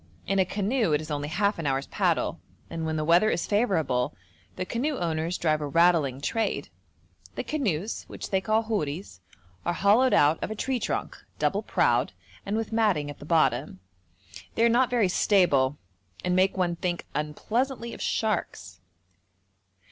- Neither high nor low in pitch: Yes, medium, 180 Hz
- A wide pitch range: Yes, wide, 6.1 semitones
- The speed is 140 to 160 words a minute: No, average, 170 wpm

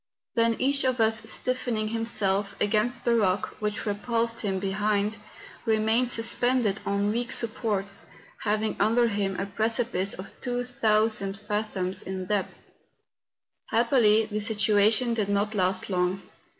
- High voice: Yes, high, 215 Hz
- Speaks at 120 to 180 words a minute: Yes, slow, 135 wpm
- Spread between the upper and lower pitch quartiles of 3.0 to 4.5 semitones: No, narrow, 2.4 semitones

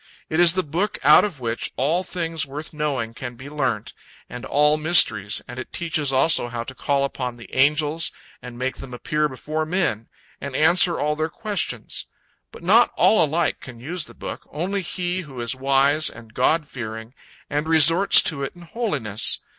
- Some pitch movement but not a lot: Yes, average, 4.5 semitones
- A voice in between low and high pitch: Yes, medium, 150 Hz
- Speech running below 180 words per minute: No, average, 185 wpm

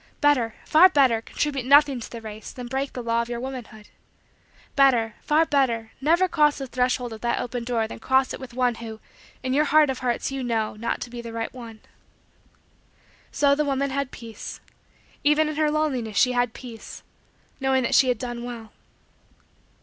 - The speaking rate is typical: Yes, average, 190 wpm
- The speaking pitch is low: No, very high, 250 Hz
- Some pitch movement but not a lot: Yes, average, 3.2 semitones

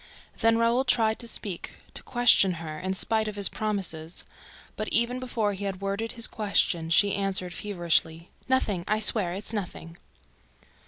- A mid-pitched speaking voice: No, high, 205 Hz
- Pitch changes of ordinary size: Yes, average, 3.8 semitones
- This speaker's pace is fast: No, average, 165 wpm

